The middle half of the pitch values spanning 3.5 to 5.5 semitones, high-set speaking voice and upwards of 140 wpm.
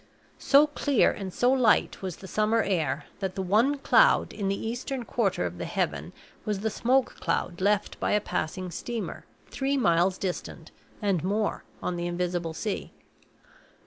Yes: average, 4.7 semitones; high, 200 Hz; average, 165 wpm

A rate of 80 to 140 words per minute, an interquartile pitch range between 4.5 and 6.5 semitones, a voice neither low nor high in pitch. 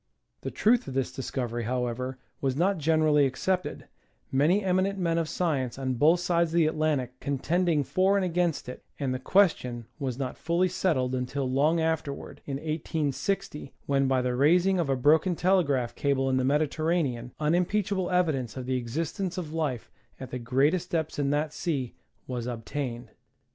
No: average, 170 wpm; average, 4.9 semitones; medium, 150 Hz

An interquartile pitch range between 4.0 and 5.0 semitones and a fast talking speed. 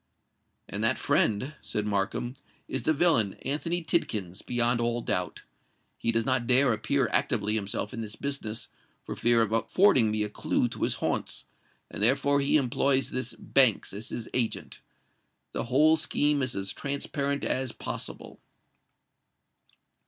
No: average, 4.4 semitones; average, 145 wpm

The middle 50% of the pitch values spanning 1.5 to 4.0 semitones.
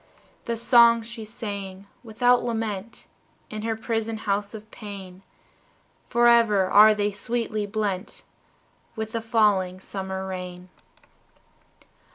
Yes: narrow, 2.6 semitones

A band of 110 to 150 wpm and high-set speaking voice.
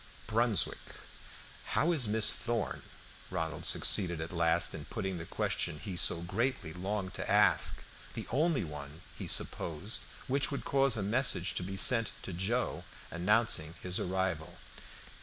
No: average, 145 wpm; very low, 95 Hz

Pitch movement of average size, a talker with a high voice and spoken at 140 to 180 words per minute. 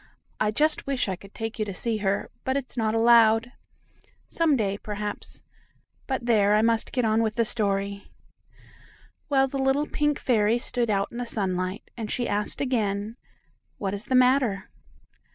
Yes: average, 3.6 semitones; high, 225 Hz; average, 170 wpm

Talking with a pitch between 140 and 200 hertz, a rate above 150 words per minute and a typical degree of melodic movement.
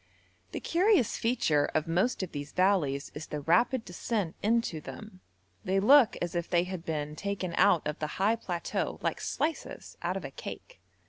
No: medium, 185 Hz; average, 180 wpm; wide, 5.9 semitones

